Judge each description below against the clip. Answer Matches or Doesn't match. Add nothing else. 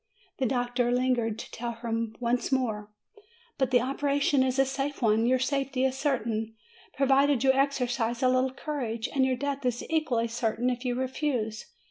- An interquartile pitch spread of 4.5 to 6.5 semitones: Doesn't match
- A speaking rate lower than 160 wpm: Doesn't match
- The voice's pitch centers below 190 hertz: Doesn't match